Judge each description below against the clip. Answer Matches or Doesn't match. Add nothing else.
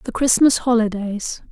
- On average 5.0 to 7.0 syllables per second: Doesn't match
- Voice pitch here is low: Doesn't match